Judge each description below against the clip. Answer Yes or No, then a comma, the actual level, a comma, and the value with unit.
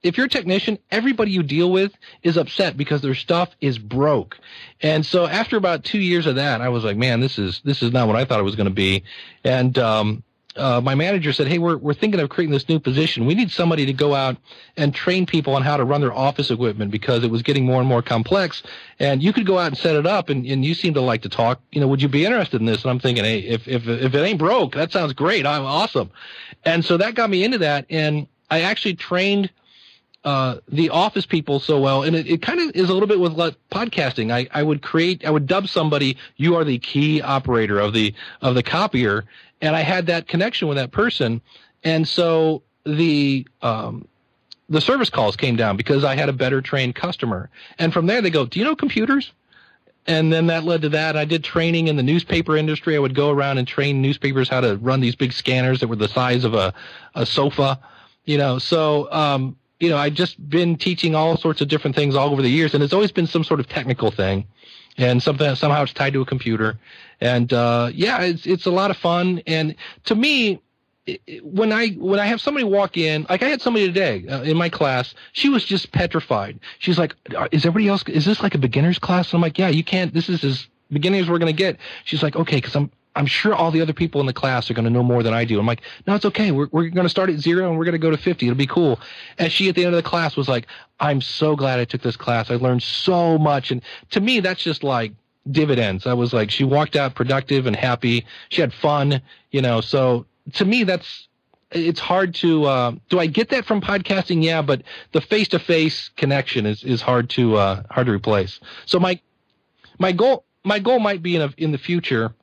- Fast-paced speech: Yes, fast, 245 wpm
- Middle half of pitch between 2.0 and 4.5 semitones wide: No, wide, 5.4 semitones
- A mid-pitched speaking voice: Yes, medium, 150 Hz